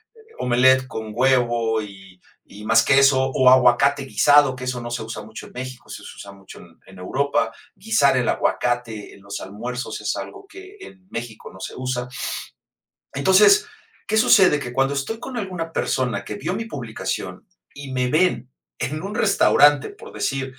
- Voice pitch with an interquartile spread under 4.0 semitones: No, average, 4.5 semitones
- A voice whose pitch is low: Yes, low, 130 Hz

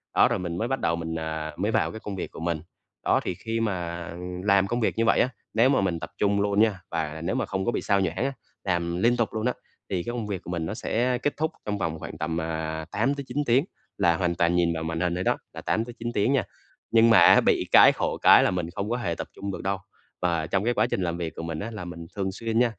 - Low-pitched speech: Yes, very low, 95 Hz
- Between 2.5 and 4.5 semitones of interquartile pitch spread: No, average, 5.1 semitones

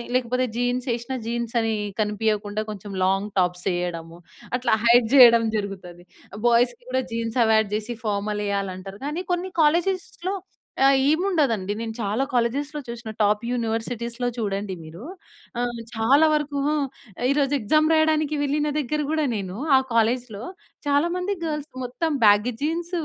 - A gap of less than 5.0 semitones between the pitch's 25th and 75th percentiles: No, wide, 5.5 semitones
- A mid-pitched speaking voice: No, high, 235 Hz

